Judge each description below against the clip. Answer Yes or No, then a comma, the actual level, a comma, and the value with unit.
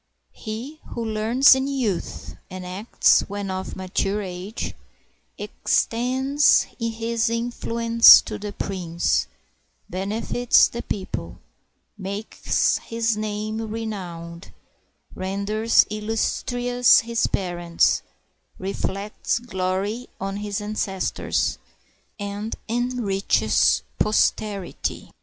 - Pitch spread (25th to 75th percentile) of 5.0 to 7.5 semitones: No, average, 3.1 semitones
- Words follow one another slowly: Yes, slow, 85 wpm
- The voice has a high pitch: Yes, high, 215 Hz